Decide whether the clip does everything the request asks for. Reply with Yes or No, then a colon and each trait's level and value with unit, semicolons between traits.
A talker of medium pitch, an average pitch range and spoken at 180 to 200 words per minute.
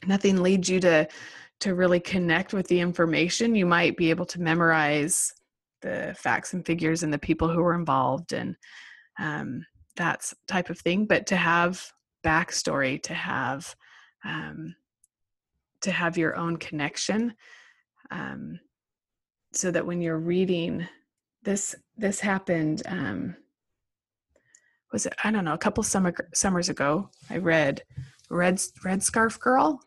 No: medium, 175 Hz; average, 3.0 semitones; average, 140 wpm